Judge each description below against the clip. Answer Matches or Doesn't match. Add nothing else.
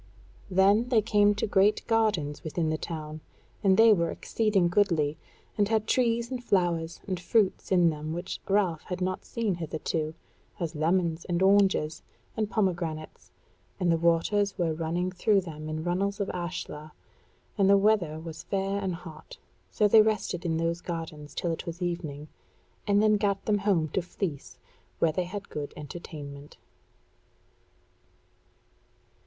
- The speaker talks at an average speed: Matches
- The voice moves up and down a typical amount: Matches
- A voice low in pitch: Doesn't match